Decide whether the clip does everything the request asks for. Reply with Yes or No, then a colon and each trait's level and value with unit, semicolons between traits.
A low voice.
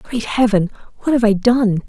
No: high, 220 Hz